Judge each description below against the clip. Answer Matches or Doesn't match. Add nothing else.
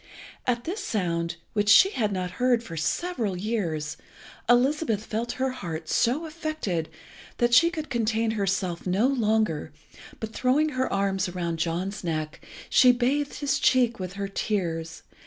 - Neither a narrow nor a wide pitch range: Doesn't match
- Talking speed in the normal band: Matches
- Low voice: Doesn't match